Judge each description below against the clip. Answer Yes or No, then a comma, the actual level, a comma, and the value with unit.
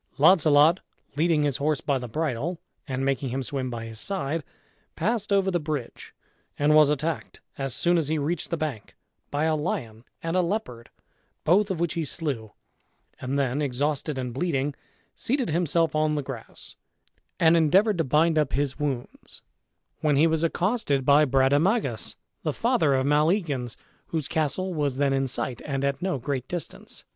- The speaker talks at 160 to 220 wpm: Yes, average, 170 wpm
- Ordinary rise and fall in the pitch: Yes, average, 3.6 semitones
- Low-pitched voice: No, medium, 150 Hz